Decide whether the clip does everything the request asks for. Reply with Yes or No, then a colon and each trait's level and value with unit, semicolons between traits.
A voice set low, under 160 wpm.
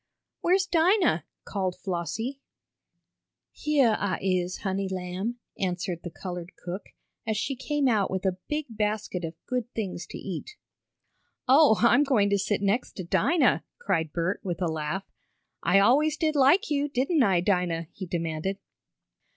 No: high, 200 Hz; average, 150 wpm